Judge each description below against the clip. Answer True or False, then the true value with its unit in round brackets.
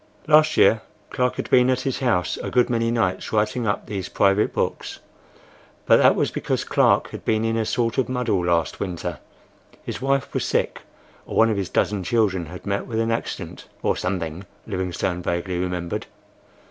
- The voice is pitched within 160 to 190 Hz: False (105 Hz)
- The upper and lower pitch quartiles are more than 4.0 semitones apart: True (4.5 semitones)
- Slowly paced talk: False (170 wpm)